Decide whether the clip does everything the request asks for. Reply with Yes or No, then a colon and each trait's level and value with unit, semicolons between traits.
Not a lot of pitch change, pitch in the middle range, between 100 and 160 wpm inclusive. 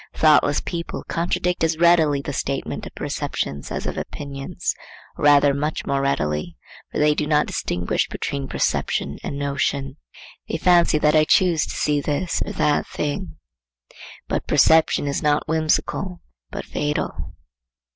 Yes: narrow, 2.3 semitones; medium, 150 Hz; average, 145 wpm